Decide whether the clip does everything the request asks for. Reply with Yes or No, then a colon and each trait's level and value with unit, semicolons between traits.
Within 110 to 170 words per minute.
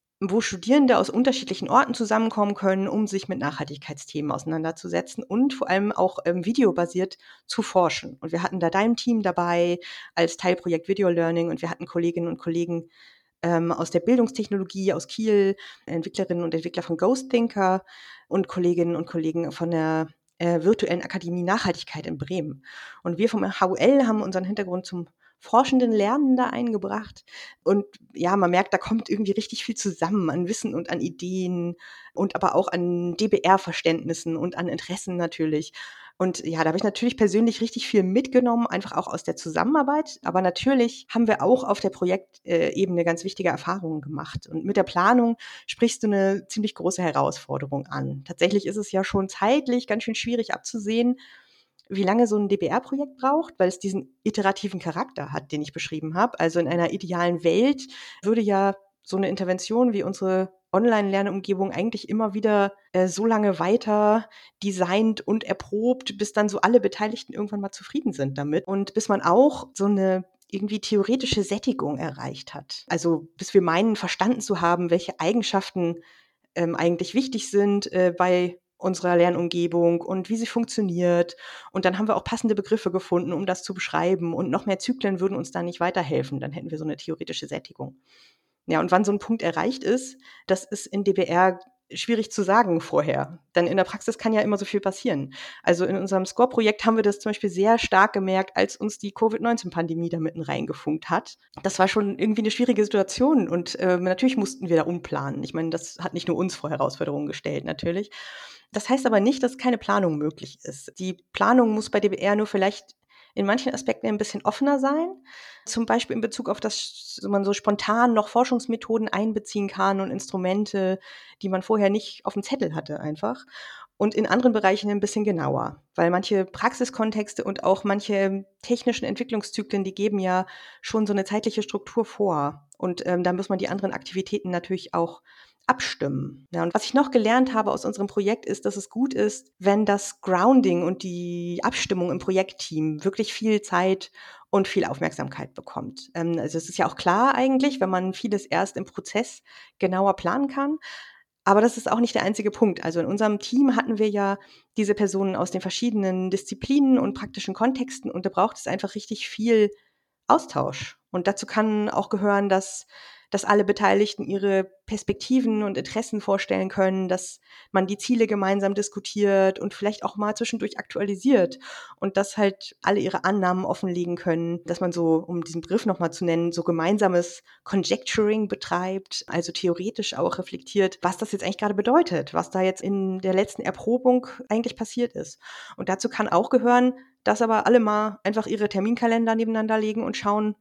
No: average, 180 wpm